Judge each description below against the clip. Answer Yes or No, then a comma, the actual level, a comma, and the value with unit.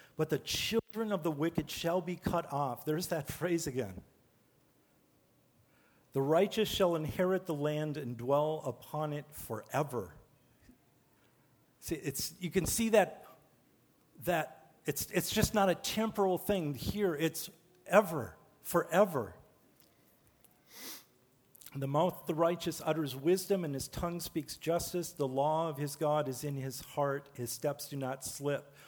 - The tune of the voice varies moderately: Yes, average, 3.8 semitones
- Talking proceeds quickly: No, average, 145 wpm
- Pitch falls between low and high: Yes, medium, 155 Hz